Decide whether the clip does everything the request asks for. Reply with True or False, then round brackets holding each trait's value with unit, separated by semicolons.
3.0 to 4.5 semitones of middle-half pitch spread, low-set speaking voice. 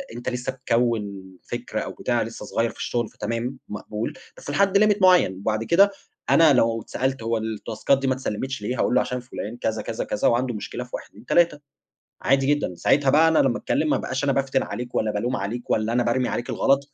True (3.3 semitones; 125 Hz)